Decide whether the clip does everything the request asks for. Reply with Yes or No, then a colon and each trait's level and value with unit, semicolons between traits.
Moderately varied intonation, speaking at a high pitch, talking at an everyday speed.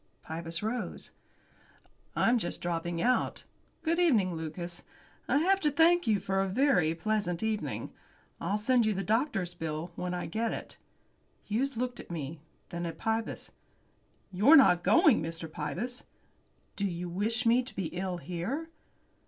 No: wide, 6.3 semitones; high, 200 Hz; average, 155 wpm